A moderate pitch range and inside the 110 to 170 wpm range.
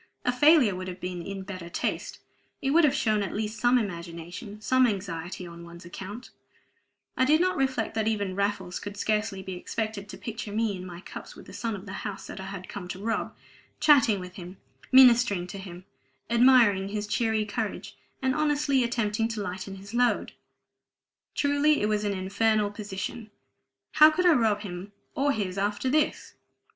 No: average, 4.2 semitones; average, 185 wpm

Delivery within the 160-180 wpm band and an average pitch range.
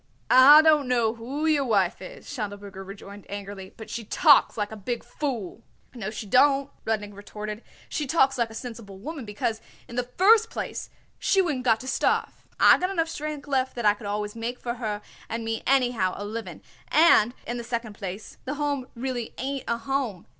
No: average, 195 wpm; average, 4.6 semitones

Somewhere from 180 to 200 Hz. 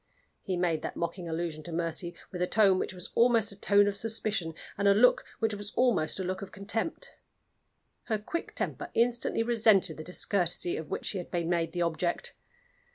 Yes: high, 190 Hz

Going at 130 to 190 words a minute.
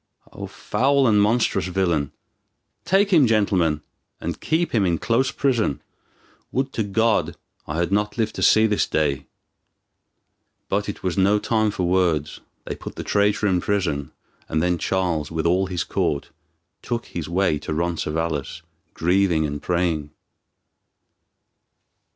Yes: average, 145 wpm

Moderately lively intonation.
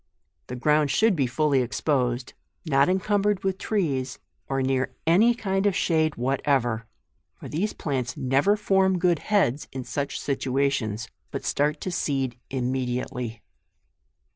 No: wide, 6.2 semitones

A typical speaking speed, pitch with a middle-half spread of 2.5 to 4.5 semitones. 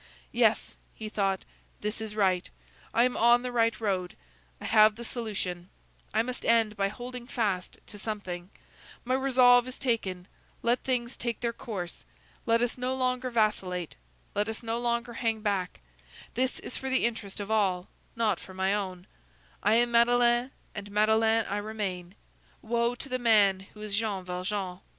Yes: average, 170 wpm; average, 3.3 semitones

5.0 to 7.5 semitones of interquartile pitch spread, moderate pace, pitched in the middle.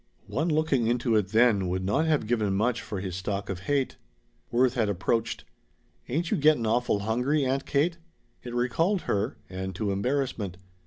No: average, 5.3 semitones; average, 170 wpm; low, 120 Hz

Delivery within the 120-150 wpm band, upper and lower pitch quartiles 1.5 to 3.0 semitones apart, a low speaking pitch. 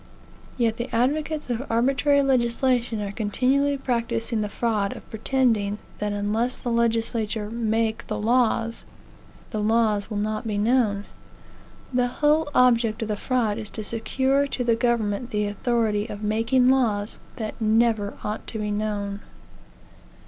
No: average, 140 wpm; average, 2.7 semitones; high, 230 Hz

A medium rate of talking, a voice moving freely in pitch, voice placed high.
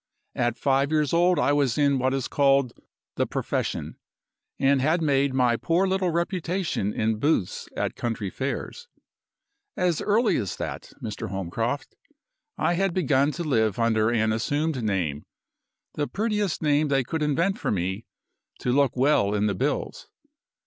No: average, 155 wpm; wide, 6.1 semitones; medium, 140 Hz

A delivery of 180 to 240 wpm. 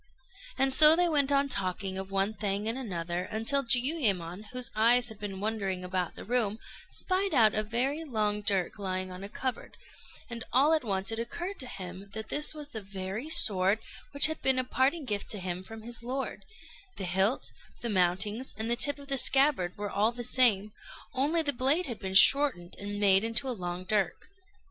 Yes: average, 200 wpm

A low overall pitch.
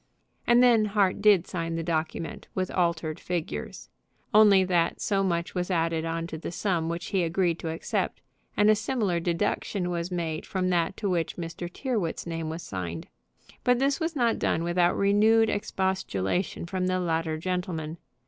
No: medium, 175 Hz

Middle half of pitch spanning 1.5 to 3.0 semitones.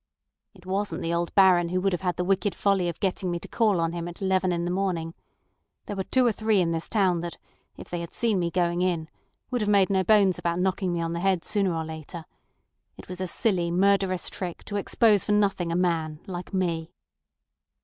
Yes: narrow, 2.4 semitones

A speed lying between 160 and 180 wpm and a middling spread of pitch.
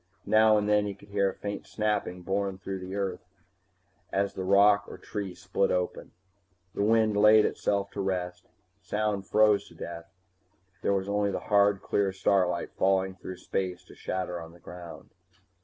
No: average, 170 wpm; narrow, 1.7 semitones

